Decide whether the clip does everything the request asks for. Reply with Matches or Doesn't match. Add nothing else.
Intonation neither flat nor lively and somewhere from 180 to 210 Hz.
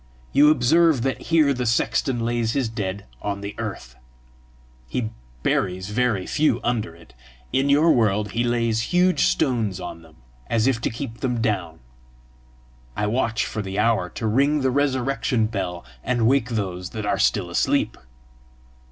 Doesn't match